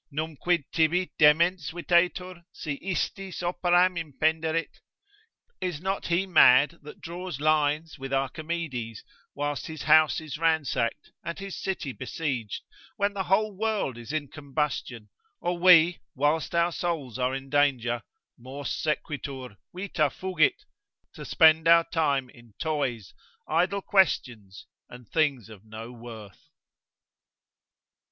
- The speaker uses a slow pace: Yes, slow, 125 wpm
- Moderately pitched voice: Yes, medium, 155 Hz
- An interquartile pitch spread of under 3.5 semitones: No, average, 4.5 semitones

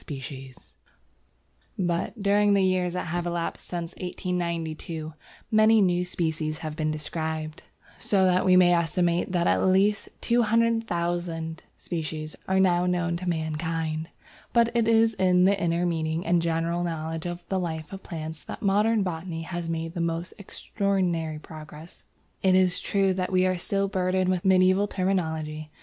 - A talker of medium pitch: Yes, medium, 175 Hz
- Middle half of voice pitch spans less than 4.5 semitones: Yes, narrow, 2.5 semitones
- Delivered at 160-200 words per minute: No, average, 150 wpm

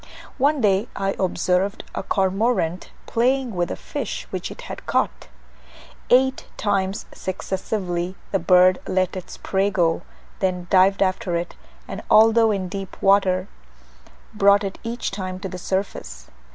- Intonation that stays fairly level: Yes, narrow, 2.0 semitones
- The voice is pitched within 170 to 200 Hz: Yes, high, 190 Hz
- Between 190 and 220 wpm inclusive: No, average, 140 wpm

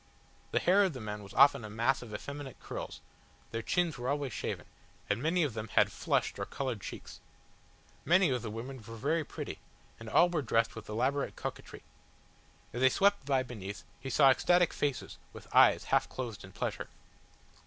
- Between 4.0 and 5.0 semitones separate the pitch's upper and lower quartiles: Yes, average, 4.4 semitones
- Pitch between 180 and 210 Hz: No, low, 130 Hz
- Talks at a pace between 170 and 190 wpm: Yes, average, 185 wpm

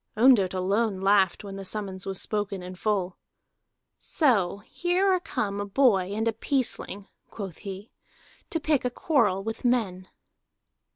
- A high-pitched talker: Yes, high, 205 Hz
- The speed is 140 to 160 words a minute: Yes, average, 150 wpm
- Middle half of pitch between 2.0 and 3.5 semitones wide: No, average, 4.1 semitones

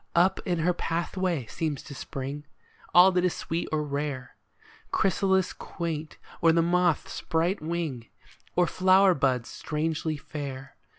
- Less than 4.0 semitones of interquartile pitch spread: Yes, average, 3.6 semitones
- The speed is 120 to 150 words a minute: Yes, average, 140 wpm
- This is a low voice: No, medium, 165 Hz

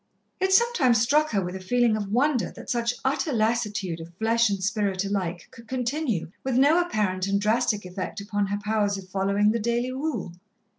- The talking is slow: No, average, 190 wpm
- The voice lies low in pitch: No, high, 215 Hz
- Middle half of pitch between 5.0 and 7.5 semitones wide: No, average, 3.9 semitones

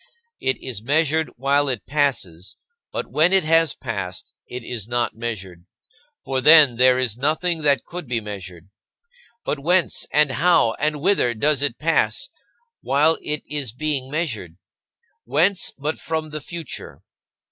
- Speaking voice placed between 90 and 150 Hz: Yes, medium, 140 Hz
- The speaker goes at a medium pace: Yes, average, 145 wpm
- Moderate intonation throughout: Yes, average, 4.8 semitones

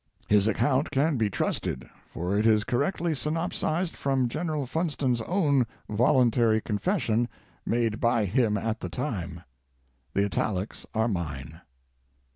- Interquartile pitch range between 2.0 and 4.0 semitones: No, average, 5.3 semitones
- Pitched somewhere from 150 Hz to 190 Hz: No, low, 120 Hz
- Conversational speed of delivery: No, slow, 130 wpm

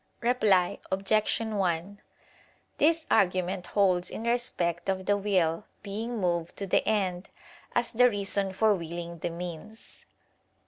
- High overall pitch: Yes, high, 195 Hz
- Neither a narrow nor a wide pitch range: Yes, average, 3.5 semitones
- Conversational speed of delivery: No, slow, 130 wpm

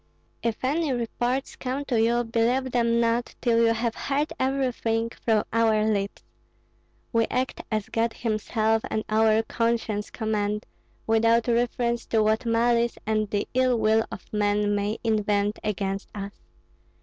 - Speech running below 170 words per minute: Yes, average, 145 wpm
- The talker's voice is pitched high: Yes, high, 230 Hz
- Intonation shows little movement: Yes, narrow, 1.8 semitones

